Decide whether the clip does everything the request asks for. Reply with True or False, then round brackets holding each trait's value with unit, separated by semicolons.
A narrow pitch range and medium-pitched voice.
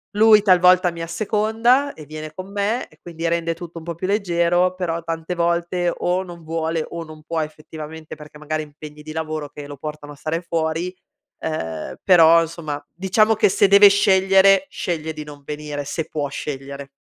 False (3.0 semitones; 165 Hz)